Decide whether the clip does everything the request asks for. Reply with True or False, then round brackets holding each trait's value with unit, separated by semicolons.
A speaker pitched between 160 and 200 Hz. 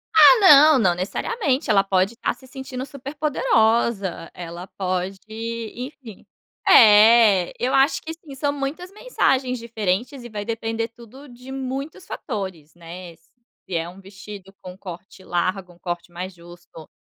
False (220 Hz)